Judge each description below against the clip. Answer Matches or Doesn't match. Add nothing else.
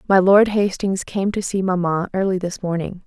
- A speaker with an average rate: Matches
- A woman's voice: Matches